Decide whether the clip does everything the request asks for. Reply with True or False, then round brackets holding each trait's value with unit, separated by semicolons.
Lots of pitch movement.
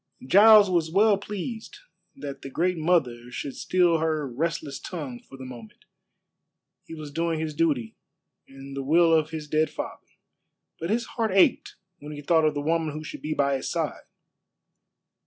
False (3.7 semitones)